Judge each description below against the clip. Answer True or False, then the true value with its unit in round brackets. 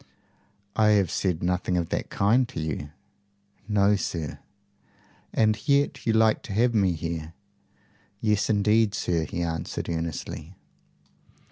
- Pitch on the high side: False (100 Hz)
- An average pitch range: True (4.5 semitones)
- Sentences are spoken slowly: True (130 wpm)